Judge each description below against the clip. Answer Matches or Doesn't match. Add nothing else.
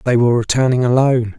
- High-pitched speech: Doesn't match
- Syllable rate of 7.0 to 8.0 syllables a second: Matches